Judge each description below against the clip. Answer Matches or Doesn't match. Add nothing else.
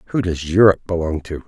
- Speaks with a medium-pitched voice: Doesn't match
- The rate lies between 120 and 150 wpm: Doesn't match